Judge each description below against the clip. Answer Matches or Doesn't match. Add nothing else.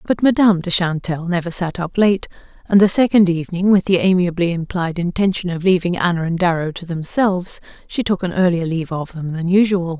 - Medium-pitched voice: Matches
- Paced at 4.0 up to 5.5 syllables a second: Doesn't match